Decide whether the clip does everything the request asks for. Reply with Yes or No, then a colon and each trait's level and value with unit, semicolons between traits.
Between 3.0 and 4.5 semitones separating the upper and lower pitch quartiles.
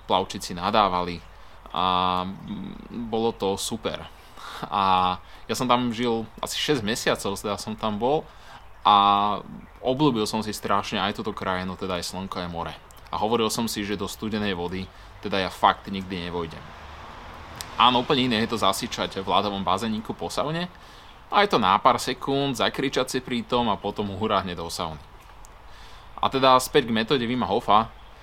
Yes: average, 4.0 semitones